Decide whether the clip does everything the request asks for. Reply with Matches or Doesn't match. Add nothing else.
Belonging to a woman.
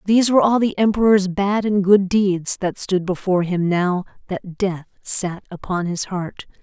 Matches